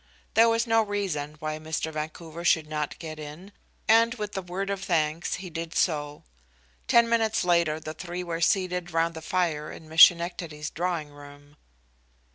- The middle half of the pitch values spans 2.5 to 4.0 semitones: Yes, average, 3.4 semitones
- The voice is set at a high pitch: No, medium, 170 Hz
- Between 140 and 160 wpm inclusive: No, average, 170 wpm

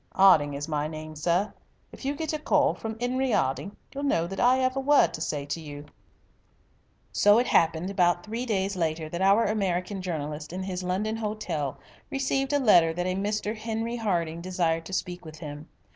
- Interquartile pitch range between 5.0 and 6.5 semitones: Yes, wide, 5.5 semitones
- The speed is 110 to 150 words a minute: No, average, 195 wpm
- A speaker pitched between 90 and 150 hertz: No, medium, 185 Hz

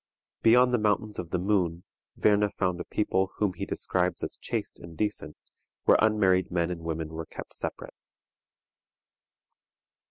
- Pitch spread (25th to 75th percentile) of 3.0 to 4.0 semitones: Yes, average, 3.6 semitones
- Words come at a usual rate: Yes, average, 150 wpm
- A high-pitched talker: No, very low, 95 Hz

